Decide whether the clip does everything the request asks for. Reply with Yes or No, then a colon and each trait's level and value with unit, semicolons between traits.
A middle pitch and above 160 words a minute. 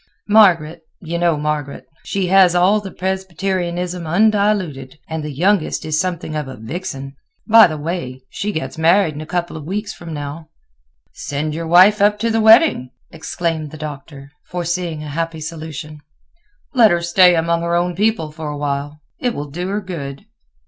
Yes: medium, 170 Hz; average, 170 wpm